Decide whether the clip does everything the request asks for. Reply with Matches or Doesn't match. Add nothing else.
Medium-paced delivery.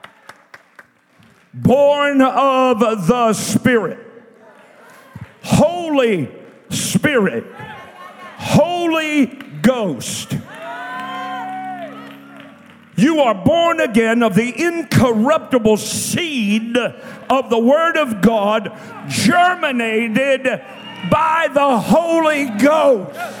Doesn't match